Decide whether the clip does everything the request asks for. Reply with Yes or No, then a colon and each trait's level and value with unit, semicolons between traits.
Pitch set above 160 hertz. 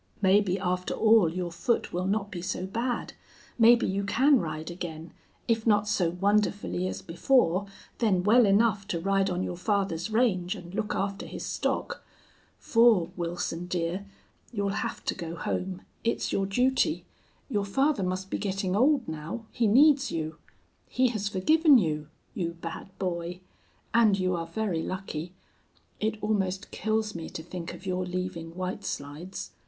Yes: high, 190 Hz